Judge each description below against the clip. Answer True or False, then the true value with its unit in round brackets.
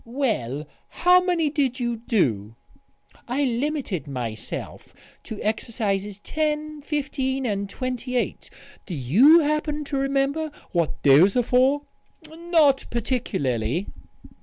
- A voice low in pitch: False (250 Hz)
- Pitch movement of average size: False (7.2 semitones)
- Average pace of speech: False (110 wpm)